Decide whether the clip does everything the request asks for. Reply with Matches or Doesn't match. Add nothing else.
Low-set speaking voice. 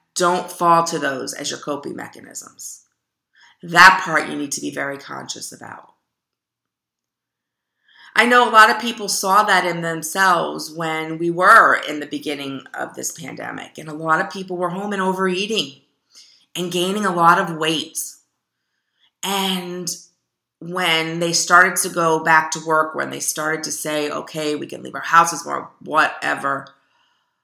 Doesn't match